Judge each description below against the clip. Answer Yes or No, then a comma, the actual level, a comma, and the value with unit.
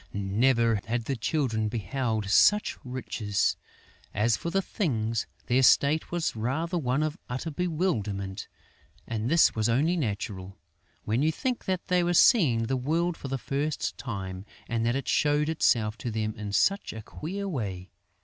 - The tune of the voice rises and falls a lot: Yes, wide, 6.7 semitones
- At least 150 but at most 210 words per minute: Yes, average, 160 wpm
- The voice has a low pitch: Yes, low, 125 Hz